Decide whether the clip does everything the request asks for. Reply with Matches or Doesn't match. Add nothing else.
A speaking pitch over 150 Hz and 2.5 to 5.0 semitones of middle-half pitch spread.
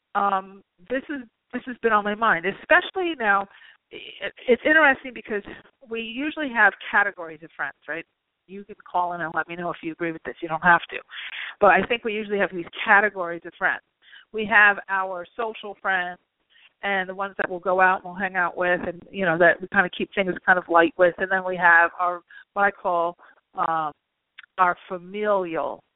Matches